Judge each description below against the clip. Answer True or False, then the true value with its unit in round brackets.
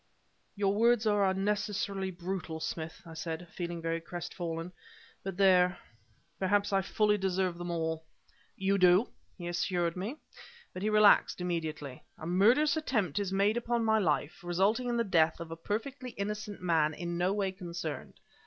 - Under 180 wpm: True (160 wpm)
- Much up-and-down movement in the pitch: False (3.4 semitones)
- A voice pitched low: False (190 Hz)